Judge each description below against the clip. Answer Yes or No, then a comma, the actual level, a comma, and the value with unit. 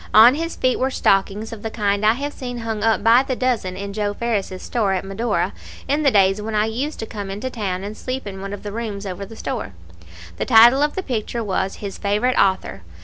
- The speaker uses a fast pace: Yes, fast, 240 wpm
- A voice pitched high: Yes, high, 215 Hz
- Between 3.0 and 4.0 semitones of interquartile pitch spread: Yes, average, 3.6 semitones